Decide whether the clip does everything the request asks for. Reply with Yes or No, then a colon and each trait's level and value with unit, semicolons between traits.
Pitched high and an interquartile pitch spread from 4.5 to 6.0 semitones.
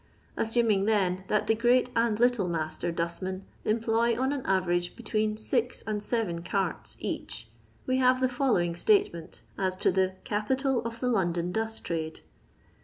Yes: high, 215 Hz; average, 5.0 semitones